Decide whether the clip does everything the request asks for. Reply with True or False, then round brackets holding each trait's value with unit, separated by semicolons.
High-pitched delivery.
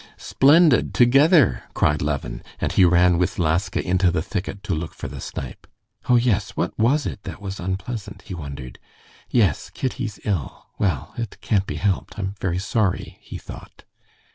False (95 Hz)